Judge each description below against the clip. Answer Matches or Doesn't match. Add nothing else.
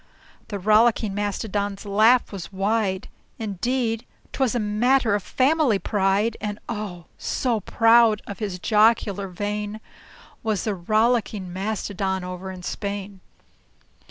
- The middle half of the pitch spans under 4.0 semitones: Matches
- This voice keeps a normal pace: Doesn't match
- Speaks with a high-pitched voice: Matches